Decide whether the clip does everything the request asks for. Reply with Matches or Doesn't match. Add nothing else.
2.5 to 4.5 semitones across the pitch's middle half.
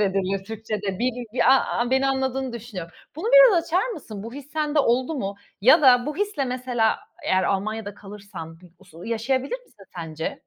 Doesn't match